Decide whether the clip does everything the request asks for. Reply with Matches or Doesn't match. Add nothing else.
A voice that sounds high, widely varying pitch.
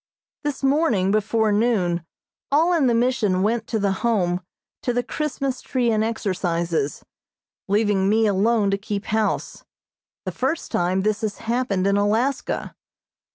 Doesn't match